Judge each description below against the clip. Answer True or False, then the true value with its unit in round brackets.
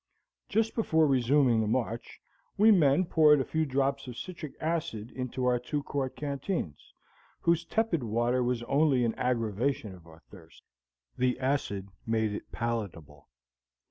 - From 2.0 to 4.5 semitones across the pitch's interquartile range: False (4.9 semitones)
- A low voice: True (130 Hz)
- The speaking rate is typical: True (145 wpm)